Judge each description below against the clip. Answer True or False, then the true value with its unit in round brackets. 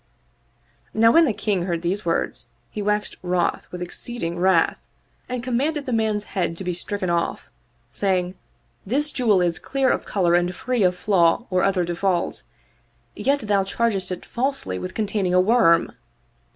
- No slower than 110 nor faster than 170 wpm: True (165 wpm)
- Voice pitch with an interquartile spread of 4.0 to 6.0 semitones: True (4.4 semitones)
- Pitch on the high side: True (195 Hz)